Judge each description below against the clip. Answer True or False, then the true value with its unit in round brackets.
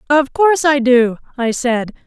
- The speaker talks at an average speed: True (175 wpm)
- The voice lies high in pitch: True (265 Hz)